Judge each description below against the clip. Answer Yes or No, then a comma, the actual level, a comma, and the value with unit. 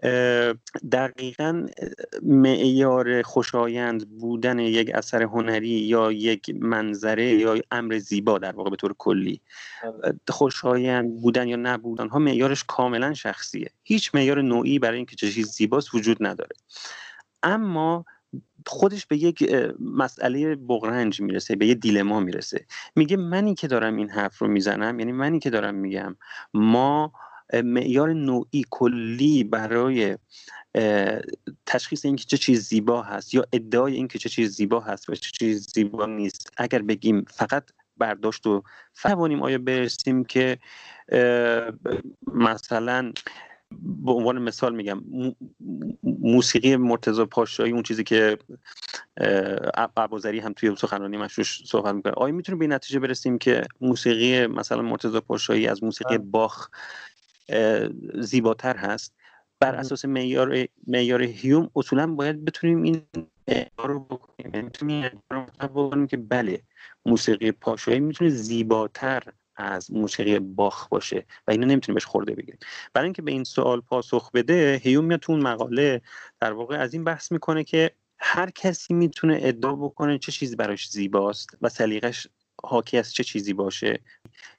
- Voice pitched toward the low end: Yes, low, 125 Hz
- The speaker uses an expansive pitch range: No, average, 3.8 semitones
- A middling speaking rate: Yes, average, 130 wpm